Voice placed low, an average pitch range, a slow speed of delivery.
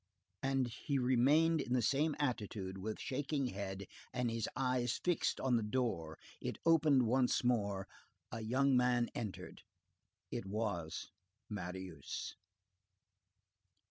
Yes: low, 120 Hz; average, 4.6 semitones; slow, 120 wpm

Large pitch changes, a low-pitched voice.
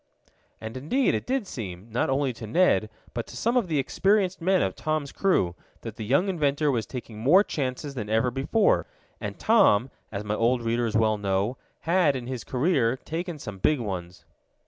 Yes: wide, 6.8 semitones; low, 130 Hz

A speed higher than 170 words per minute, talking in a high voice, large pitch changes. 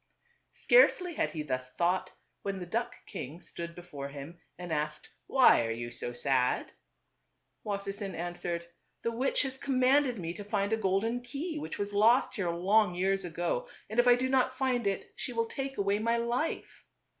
Yes: average, 190 wpm; high, 200 Hz; wide, 6.2 semitones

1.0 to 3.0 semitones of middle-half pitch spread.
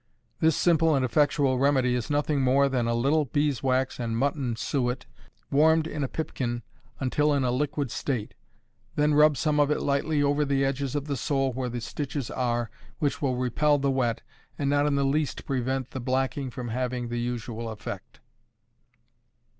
Yes: average, 2.7 semitones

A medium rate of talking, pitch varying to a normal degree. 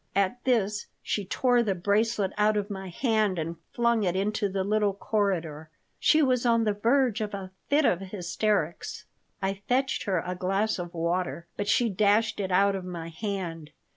Yes: average, 180 wpm; average, 3.1 semitones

